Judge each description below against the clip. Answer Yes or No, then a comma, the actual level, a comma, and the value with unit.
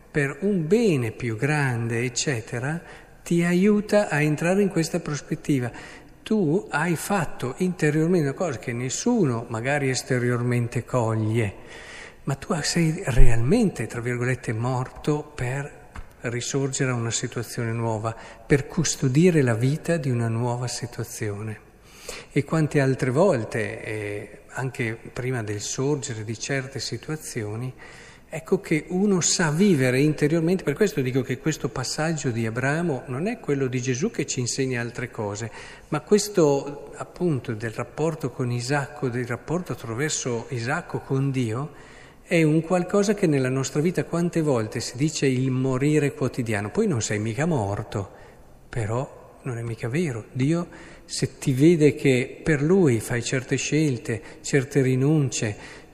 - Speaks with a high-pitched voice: No, low, 135 Hz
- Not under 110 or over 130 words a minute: No, average, 140 wpm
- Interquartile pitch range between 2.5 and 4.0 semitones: No, average, 4.6 semitones